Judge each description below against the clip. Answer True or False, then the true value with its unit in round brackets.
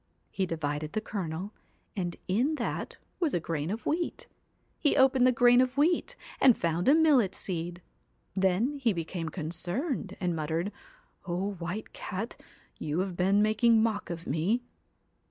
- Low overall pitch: False (195 Hz)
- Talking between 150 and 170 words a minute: True (160 wpm)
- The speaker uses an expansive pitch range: True (6.2 semitones)